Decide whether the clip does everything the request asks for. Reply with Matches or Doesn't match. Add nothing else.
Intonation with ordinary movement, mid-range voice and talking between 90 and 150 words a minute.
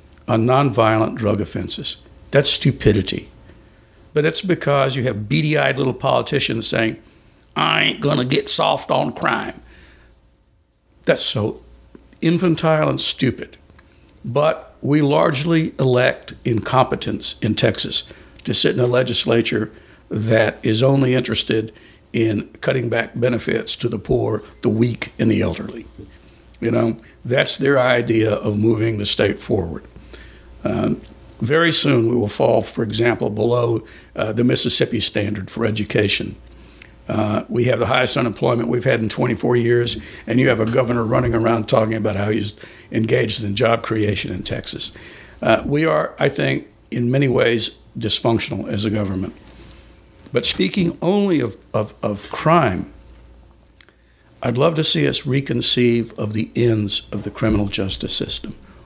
Doesn't match